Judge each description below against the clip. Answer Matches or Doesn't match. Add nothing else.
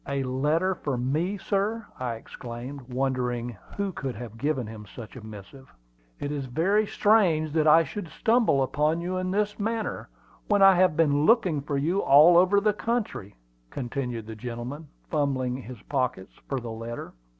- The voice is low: Doesn't match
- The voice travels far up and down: Matches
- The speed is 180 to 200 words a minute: Doesn't match